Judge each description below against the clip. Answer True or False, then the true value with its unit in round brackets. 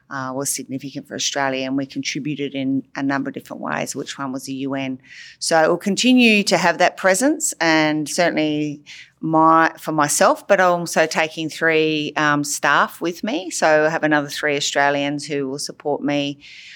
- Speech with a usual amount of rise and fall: True (3.1 semitones)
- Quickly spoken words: False (180 wpm)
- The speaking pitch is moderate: True (150 Hz)